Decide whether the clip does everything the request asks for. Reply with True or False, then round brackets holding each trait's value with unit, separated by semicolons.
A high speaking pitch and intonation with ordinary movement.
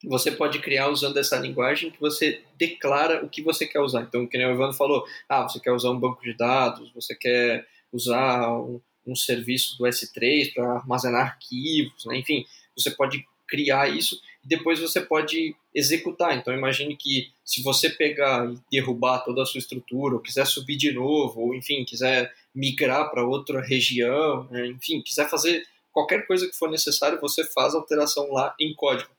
False (135 Hz; 3.3 semitones)